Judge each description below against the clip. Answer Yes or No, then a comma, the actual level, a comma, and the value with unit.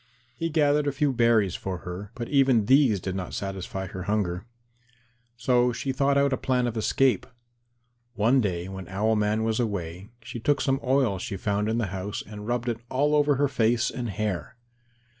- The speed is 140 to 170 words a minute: No, average, 190 wpm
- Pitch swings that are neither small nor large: Yes, average, 4.9 semitones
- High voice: No, low, 115 Hz